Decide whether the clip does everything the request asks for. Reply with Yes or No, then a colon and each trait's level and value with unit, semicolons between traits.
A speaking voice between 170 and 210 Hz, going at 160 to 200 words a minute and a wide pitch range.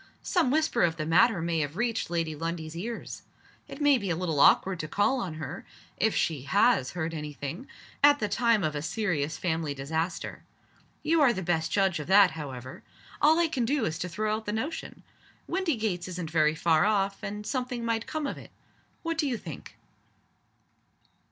Yes: medium, 185 Hz; average, 190 wpm; wide, 6.7 semitones